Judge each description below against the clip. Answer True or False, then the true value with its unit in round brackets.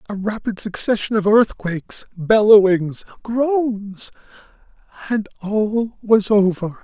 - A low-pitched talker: False (210 Hz)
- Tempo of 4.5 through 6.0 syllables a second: False (3.7 syllables/s)